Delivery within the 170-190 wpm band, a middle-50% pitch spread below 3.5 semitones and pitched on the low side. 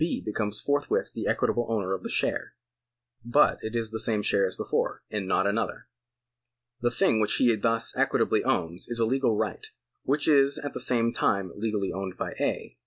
Yes: average, 185 wpm; average, 2.9 semitones; low, 110 Hz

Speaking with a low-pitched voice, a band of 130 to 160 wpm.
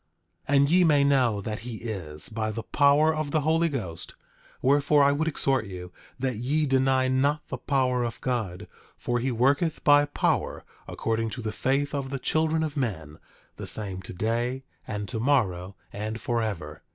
No: low, 130 Hz; average, 175 wpm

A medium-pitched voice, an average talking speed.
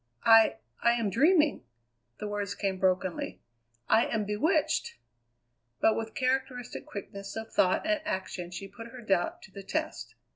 No: high, 220 Hz; average, 150 wpm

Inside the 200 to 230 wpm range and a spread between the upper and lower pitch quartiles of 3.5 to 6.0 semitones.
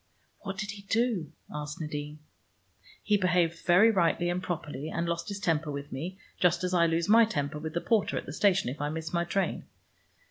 Yes: fast, 205 wpm; average, 4.1 semitones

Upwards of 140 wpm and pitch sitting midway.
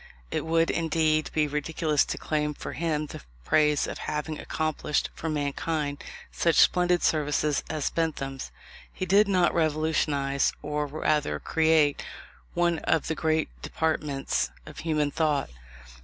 No: slow, 135 wpm; medium, 155 Hz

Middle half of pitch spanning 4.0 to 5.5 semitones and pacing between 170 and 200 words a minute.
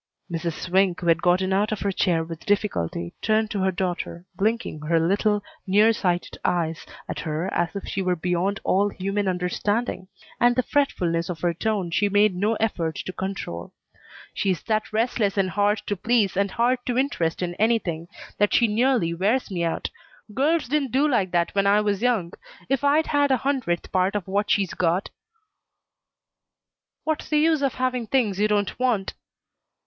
Yes: average, 4.3 semitones; average, 185 wpm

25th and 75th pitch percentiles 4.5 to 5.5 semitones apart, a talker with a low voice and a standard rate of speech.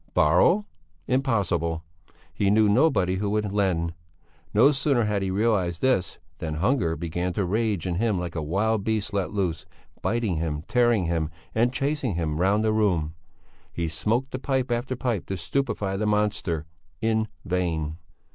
Yes: average, 4.9 semitones; low, 100 Hz; average, 155 wpm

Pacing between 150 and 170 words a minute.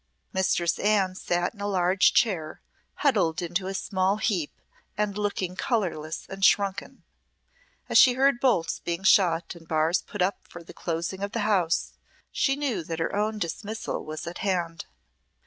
Yes: average, 165 wpm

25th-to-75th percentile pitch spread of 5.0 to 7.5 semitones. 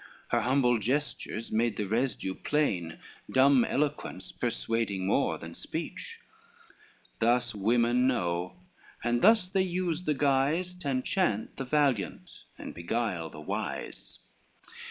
Yes: wide, 5.4 semitones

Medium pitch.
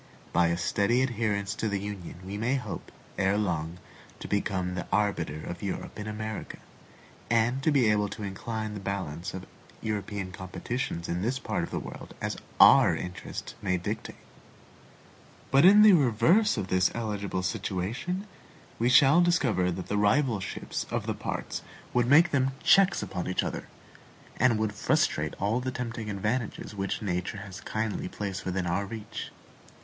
No: low, 105 Hz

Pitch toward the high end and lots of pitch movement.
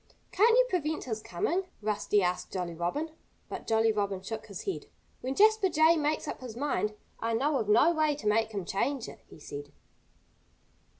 Yes: high, 225 Hz; wide, 7.3 semitones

